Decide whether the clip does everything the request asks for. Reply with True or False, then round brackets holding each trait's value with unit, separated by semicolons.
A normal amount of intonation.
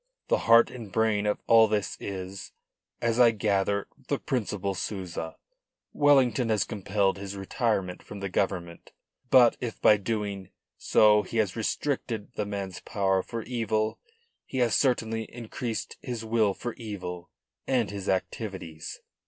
True (3.0 semitones)